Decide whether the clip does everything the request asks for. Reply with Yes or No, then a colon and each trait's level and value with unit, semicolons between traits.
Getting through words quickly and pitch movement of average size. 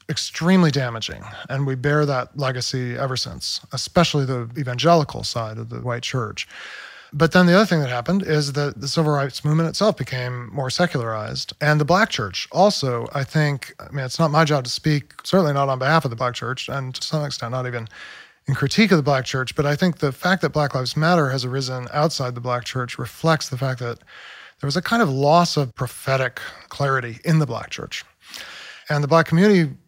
Yes: fast, 210 wpm; average, 4.1 semitones